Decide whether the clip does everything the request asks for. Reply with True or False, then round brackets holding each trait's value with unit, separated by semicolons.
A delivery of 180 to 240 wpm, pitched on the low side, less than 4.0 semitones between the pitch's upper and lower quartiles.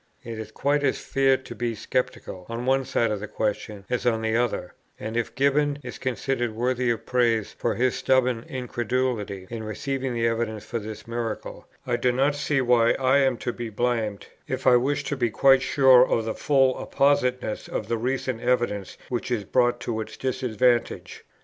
True (190 wpm; 120 Hz; 2.6 semitones)